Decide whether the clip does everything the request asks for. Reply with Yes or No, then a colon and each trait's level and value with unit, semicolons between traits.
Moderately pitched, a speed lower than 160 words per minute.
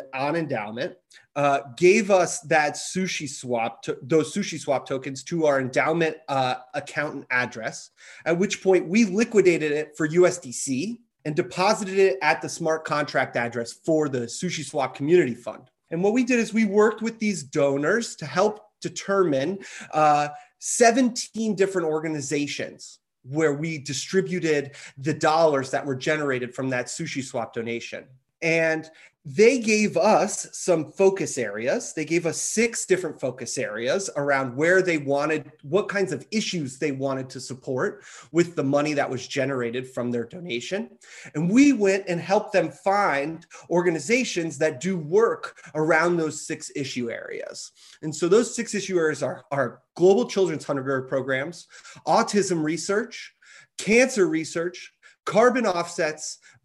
Yes: medium, 160 Hz; average, 145 wpm